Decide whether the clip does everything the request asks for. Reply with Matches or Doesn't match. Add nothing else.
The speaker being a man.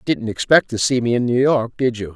Matches